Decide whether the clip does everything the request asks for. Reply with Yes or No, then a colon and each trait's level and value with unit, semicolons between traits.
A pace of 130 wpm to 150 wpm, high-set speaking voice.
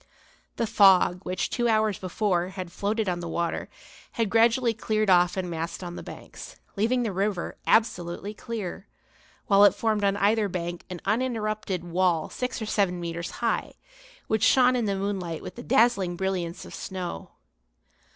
No: average, 165 wpm; high, 195 Hz